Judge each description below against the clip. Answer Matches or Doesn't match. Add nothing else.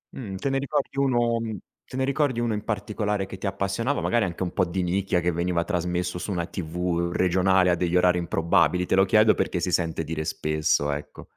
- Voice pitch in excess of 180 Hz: Doesn't match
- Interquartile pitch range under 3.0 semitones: Doesn't match